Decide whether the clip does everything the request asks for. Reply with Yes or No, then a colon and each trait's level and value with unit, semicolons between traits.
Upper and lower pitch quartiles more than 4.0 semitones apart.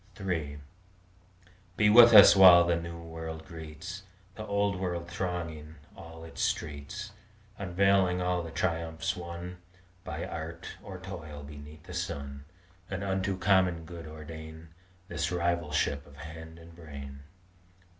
No: average, 2.7 semitones